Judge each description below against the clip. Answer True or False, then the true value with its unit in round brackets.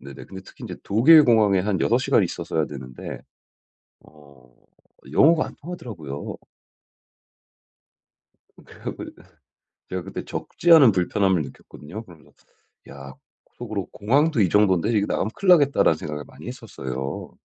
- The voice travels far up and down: True (8.3 semitones)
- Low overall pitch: True (95 Hz)